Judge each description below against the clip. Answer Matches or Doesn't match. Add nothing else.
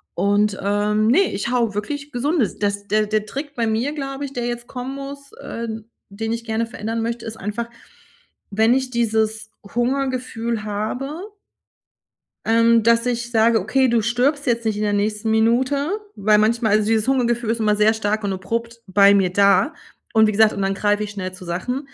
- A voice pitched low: Doesn't match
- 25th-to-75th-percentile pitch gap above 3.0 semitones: Doesn't match